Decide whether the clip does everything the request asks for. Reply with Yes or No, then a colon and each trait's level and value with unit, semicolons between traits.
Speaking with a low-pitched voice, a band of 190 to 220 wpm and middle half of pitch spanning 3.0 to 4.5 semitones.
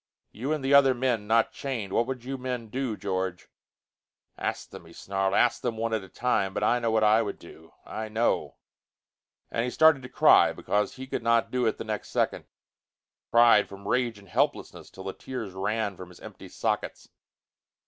Yes: low, 115 Hz; average, 200 wpm; average, 3.8 semitones